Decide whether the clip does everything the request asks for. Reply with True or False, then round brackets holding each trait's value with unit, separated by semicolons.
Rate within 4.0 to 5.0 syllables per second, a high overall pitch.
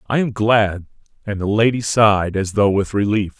False (4.9 syllables/s; 105 Hz)